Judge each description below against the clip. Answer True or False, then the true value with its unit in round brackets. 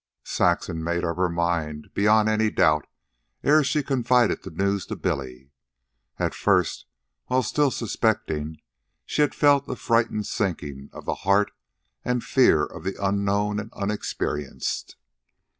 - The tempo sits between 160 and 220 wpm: False (140 wpm)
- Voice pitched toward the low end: True (100 Hz)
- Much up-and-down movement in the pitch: True (5.9 semitones)